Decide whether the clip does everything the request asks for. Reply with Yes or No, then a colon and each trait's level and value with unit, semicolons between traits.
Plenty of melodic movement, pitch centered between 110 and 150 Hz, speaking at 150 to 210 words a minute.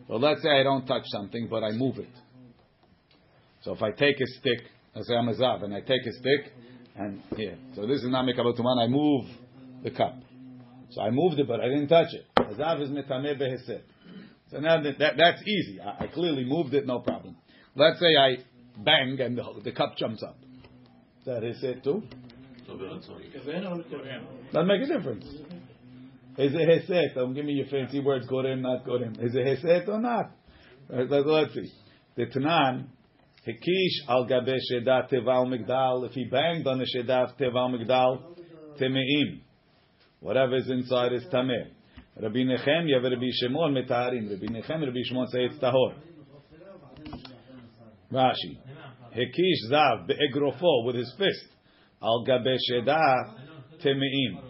No: narrow, 2.5 semitones; low, 130 Hz; average, 160 wpm